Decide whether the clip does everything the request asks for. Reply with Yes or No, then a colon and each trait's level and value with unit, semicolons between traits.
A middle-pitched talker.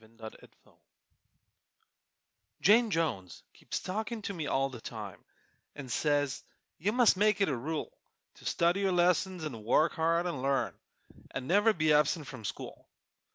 Yes: medium, 160 Hz